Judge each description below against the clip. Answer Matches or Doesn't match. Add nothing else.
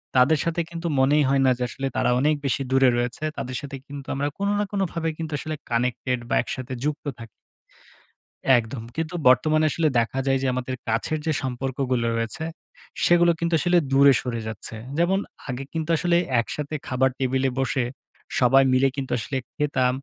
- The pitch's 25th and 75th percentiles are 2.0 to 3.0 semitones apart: Doesn't match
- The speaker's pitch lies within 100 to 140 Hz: Matches